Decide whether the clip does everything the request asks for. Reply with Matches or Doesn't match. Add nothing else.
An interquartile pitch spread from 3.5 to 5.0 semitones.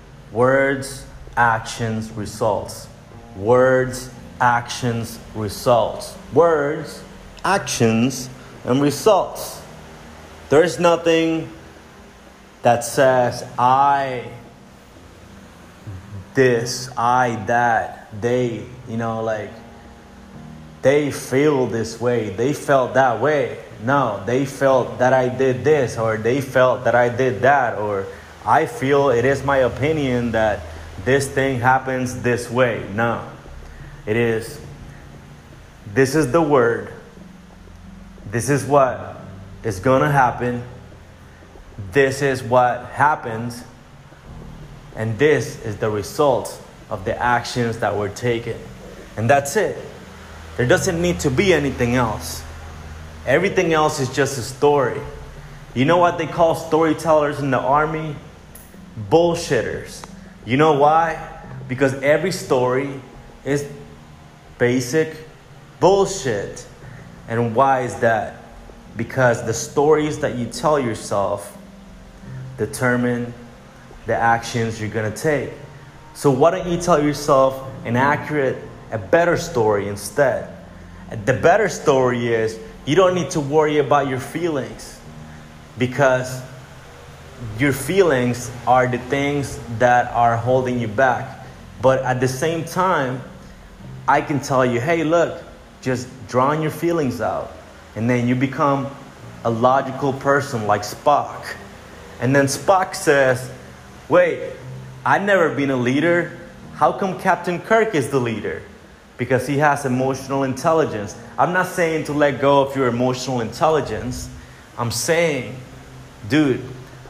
Matches